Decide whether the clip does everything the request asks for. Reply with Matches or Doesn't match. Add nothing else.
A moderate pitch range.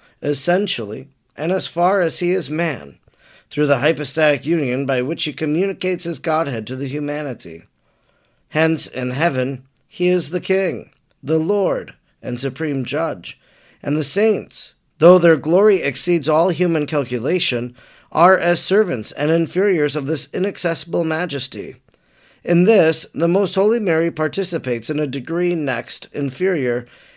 Matches